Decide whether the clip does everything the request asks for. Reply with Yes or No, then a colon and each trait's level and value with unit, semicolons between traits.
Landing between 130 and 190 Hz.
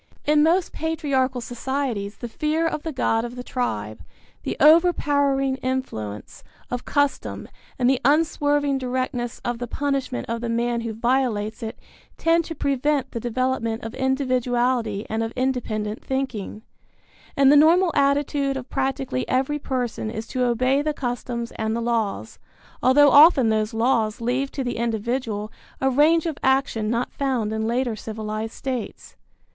No: very high, 255 Hz